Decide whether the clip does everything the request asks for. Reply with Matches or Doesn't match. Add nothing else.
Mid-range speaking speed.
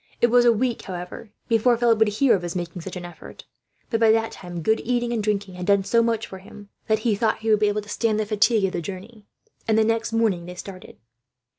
Doesn't match